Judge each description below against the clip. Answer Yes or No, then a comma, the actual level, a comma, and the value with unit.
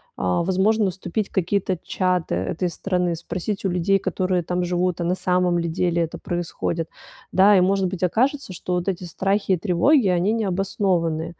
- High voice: No, medium, 180 Hz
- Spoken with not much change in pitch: Yes, narrow, 2.1 semitones